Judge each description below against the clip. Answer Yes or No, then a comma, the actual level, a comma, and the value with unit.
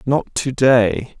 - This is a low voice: Yes, low, 125 Hz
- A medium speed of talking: Yes, average, 150 wpm